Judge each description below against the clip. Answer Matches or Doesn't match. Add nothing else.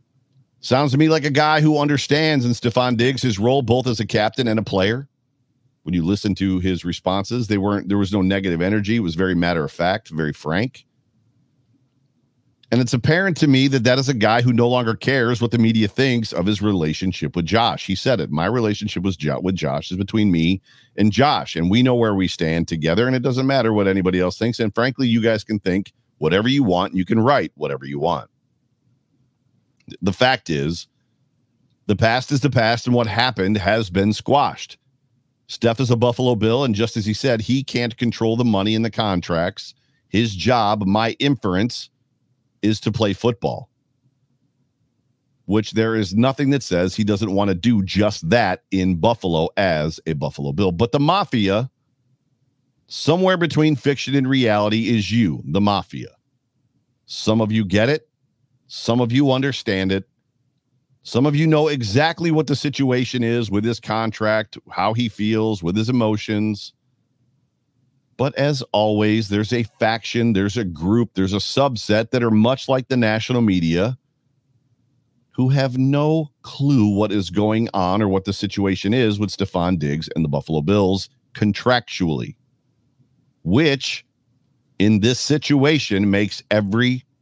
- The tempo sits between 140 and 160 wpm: Doesn't match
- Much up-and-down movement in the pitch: Doesn't match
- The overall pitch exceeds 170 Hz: Doesn't match